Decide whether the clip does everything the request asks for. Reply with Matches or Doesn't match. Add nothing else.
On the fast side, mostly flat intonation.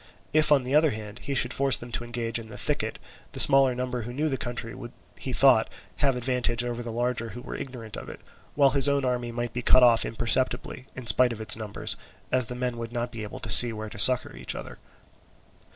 Matches